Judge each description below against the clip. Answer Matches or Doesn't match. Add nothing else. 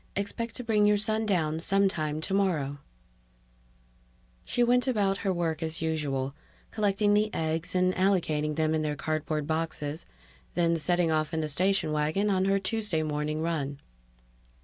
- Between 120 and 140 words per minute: Doesn't match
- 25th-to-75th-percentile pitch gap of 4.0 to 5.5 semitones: Matches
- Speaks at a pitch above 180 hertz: Doesn't match